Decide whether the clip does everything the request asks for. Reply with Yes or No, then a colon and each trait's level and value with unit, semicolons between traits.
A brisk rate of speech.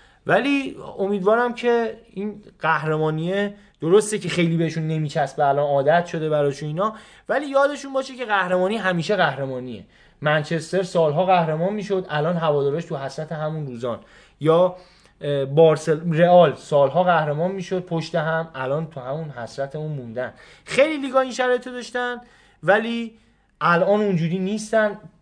No: average, 130 wpm